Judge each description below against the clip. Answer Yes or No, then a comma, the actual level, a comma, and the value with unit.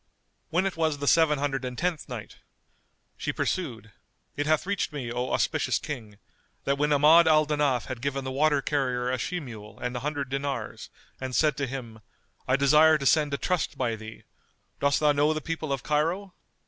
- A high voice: No, medium, 140 Hz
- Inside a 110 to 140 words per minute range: No, average, 195 wpm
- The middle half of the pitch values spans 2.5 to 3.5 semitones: Yes, average, 3.2 semitones